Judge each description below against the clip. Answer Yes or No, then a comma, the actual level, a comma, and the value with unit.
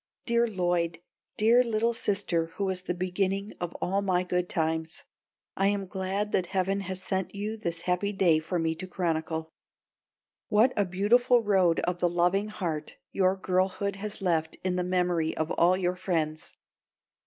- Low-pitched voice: No, medium, 185 Hz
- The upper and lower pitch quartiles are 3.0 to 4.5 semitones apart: No, narrow, 2.4 semitones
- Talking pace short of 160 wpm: No, average, 165 wpm